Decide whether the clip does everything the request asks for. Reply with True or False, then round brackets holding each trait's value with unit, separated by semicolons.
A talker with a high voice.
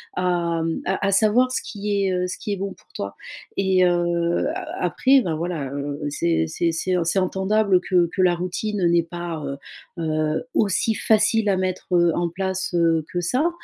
False (180 Hz)